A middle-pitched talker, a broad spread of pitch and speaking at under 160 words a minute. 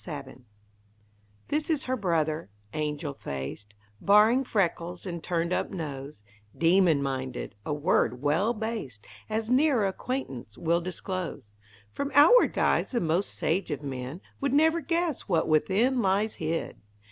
Yes: medium, 175 Hz; wide, 7.3 semitones; slow, 135 wpm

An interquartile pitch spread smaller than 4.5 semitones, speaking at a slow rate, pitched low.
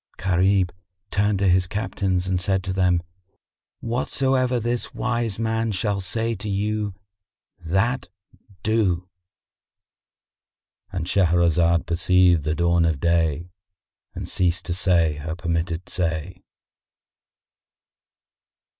Yes: average, 3.2 semitones; slow, 100 wpm; very low, 95 Hz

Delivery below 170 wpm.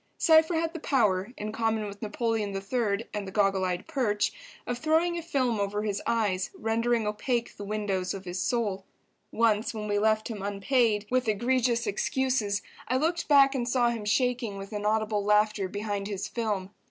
No: average, 175 wpm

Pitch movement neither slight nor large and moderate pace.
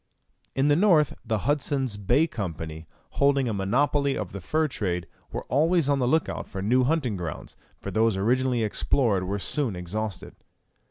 No: wide, 6.4 semitones; average, 170 wpm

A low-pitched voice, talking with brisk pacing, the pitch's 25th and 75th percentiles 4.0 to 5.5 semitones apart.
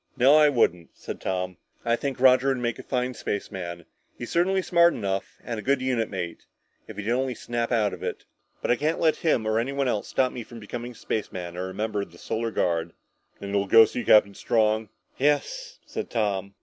Yes: low, 115 Hz; fast, 215 wpm; average, 4.6 semitones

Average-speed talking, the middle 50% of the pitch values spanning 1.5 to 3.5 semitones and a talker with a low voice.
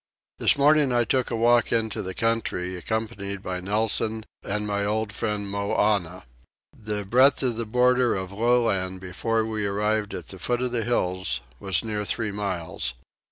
Yes: average, 170 wpm; average, 2.9 semitones; low, 105 Hz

